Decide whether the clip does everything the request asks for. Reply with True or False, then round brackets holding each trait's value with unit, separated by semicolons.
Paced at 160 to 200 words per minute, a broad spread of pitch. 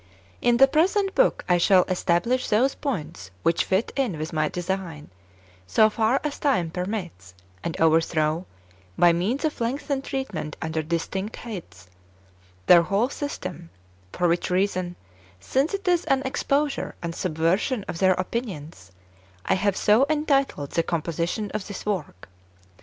False (150 wpm; 7.6 semitones)